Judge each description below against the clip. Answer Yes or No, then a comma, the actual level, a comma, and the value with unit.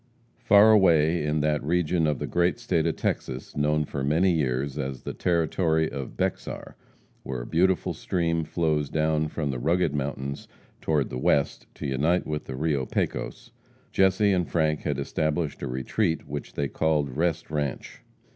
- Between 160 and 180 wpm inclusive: Yes, average, 165 wpm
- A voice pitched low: Yes, very low, 75 Hz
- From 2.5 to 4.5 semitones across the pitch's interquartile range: Yes, average, 2.9 semitones